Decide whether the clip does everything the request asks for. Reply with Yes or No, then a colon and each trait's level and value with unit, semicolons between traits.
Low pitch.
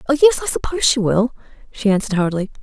No: high, 200 Hz